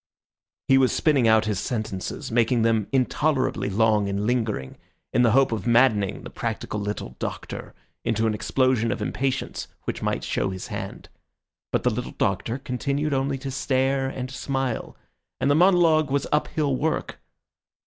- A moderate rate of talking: Yes, average, 160 wpm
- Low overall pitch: Yes, low, 125 Hz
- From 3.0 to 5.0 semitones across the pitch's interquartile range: Yes, average, 3.7 semitones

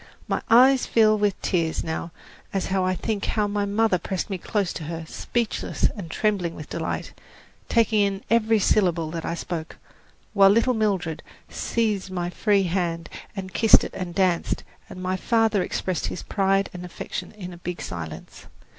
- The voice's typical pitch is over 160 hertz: Yes, high, 190 Hz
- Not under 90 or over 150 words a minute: No, average, 170 wpm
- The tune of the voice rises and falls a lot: No, average, 3.5 semitones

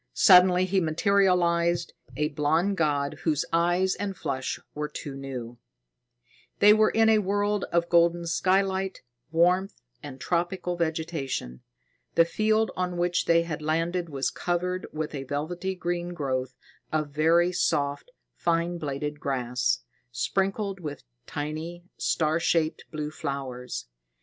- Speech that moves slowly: Yes, slow, 130 wpm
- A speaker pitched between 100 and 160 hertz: No, medium, 170 Hz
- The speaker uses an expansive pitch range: No, average, 3.6 semitones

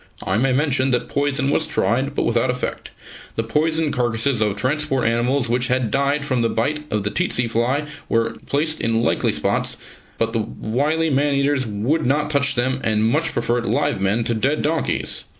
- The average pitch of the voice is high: No, low, 130 Hz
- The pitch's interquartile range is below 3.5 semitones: No, average, 3.9 semitones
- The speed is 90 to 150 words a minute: No, average, 185 wpm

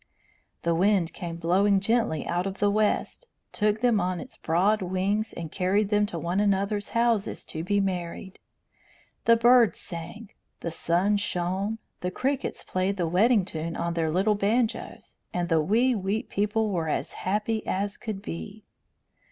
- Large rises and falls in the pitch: No, average, 3.3 semitones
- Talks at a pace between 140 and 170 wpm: Yes, average, 160 wpm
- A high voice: Yes, high, 200 Hz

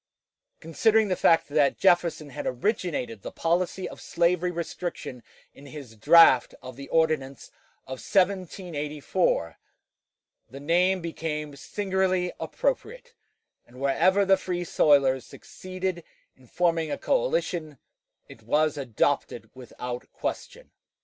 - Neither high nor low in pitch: Yes, medium, 165 Hz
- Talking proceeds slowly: Yes, slow, 115 wpm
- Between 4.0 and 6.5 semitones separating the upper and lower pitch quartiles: Yes, average, 5.0 semitones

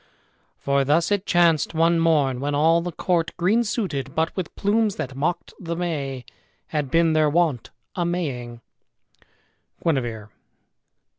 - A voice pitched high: No, medium, 165 Hz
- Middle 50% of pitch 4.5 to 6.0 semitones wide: No, average, 3.9 semitones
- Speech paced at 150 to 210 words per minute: No, average, 140 wpm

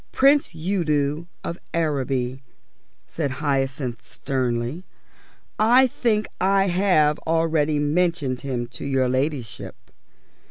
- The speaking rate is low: Yes, slow, 95 wpm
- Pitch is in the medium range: Yes, medium, 150 Hz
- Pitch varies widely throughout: No, average, 4.9 semitones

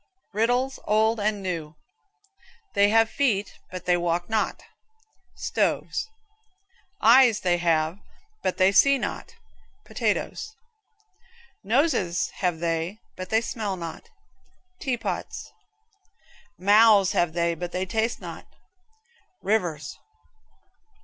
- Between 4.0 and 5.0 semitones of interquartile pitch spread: Yes, average, 4.3 semitones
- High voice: Yes, high, 195 Hz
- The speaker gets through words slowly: Yes, slow, 105 wpm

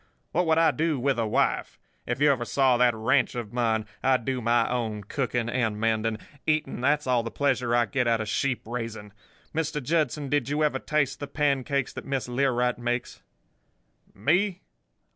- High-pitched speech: No, low, 125 Hz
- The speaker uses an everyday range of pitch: Yes, average, 3.6 semitones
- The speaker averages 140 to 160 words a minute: No, average, 180 wpm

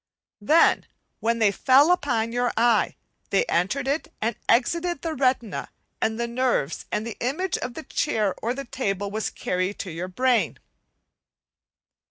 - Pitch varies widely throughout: No, average, 4.4 semitones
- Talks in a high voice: Yes, high, 235 Hz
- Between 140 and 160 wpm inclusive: Yes, average, 155 wpm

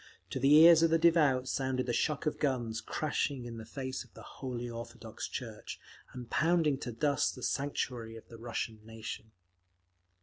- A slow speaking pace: No, average, 175 wpm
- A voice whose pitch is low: Yes, low, 130 Hz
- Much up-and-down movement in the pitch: No, average, 4.1 semitones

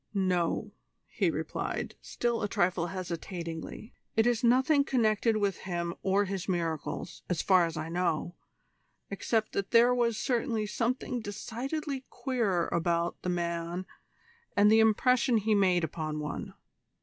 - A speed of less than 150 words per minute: Yes, slow, 135 wpm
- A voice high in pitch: Yes, high, 200 Hz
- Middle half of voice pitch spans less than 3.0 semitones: No, average, 5.3 semitones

